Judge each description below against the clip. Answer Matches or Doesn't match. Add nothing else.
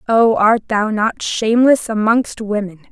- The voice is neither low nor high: Doesn't match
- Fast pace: Doesn't match